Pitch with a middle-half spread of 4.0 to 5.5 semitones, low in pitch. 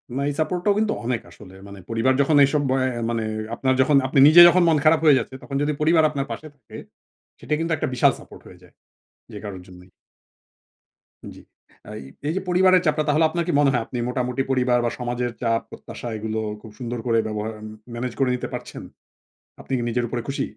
Yes: average, 4.6 semitones; low, 130 Hz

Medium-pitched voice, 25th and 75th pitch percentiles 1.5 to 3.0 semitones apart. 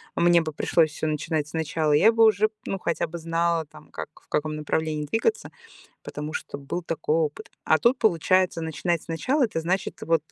Yes: medium, 165 Hz; narrow, 2.6 semitones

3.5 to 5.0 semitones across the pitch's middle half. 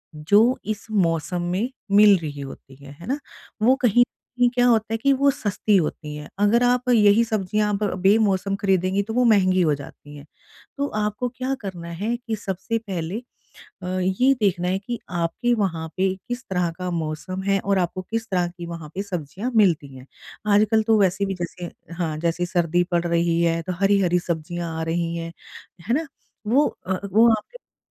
Yes: average, 4.3 semitones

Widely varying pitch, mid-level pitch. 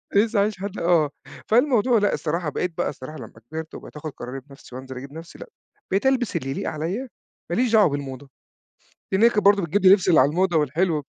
Yes: wide, 5.8 semitones; medium, 170 Hz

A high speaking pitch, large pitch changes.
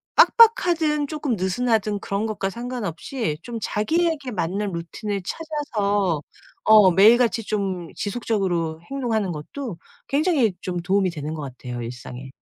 Yes: high, 210 Hz; wide, 6.0 semitones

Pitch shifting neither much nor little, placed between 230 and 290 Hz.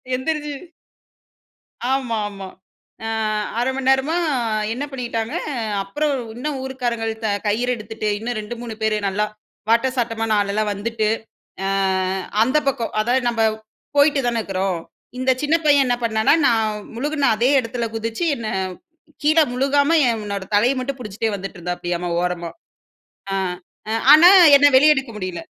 Yes: average, 3.9 semitones; high, 235 Hz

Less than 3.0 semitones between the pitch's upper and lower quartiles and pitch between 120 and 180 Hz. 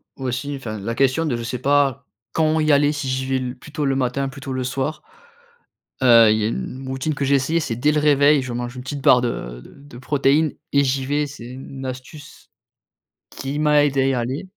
Yes: narrow, 2.5 semitones; low, 135 Hz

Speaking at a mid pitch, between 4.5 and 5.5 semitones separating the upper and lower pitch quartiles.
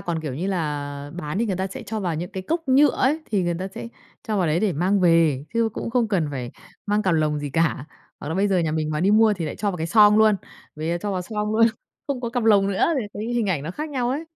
No: high, 195 Hz; average, 5.0 semitones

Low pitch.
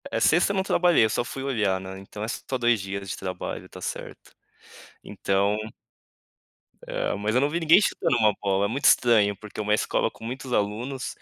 Yes: low, 110 Hz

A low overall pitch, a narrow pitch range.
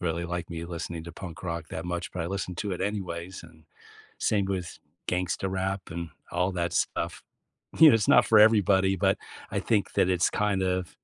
Yes: very low, 90 Hz; narrow, 2.2 semitones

